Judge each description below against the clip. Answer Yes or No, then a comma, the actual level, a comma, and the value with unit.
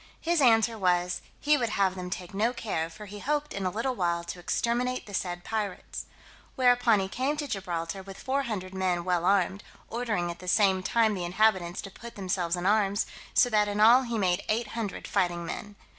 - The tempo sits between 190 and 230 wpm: Yes, fast, 205 wpm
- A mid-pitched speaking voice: No, high, 200 Hz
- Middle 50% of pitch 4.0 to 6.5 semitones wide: Yes, average, 4.3 semitones